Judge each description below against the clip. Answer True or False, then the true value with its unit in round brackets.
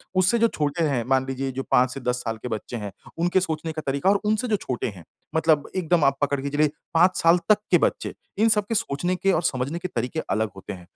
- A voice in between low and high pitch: True (155 Hz)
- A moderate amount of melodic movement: False (5.7 semitones)